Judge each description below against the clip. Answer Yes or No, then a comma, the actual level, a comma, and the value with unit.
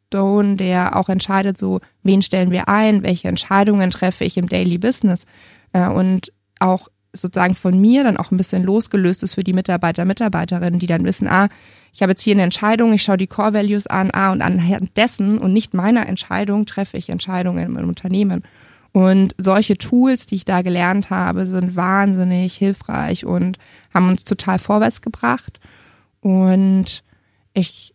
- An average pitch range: No, narrow, 1.8 semitones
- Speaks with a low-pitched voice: No, high, 190 Hz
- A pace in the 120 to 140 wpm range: No, average, 170 wpm